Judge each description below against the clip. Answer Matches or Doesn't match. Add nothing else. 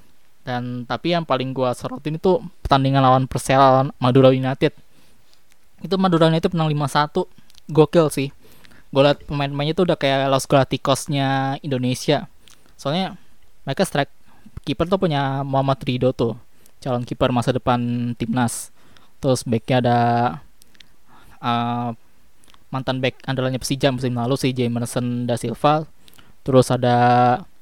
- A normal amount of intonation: Matches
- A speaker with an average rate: Matches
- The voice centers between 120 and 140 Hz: Matches